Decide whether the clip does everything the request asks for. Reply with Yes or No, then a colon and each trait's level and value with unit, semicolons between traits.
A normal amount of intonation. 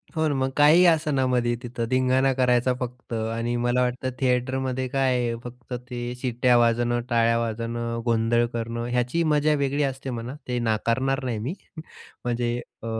No: narrow, 1.9 semitones